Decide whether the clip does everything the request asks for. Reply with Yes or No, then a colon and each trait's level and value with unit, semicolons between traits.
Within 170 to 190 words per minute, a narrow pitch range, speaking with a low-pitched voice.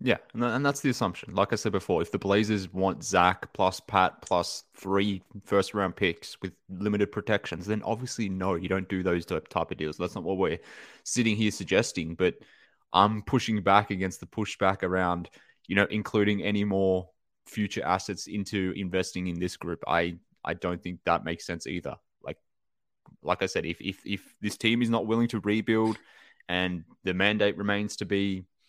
Yes: average, 185 wpm; narrow, 2.3 semitones; low, 100 Hz